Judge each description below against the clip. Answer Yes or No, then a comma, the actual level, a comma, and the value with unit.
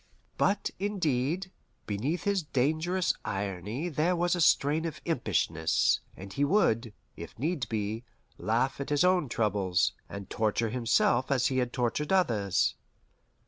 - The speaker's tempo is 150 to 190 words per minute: No, average, 140 wpm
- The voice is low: Yes, low, 130 Hz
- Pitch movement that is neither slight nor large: No, wide, 7.4 semitones